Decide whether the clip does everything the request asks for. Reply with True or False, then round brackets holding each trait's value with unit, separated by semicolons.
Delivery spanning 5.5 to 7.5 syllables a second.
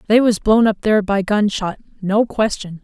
False (5.0 syllables/s)